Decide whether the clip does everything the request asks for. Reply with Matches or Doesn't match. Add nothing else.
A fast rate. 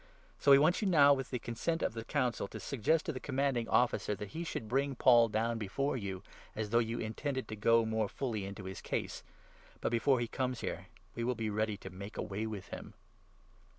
Matches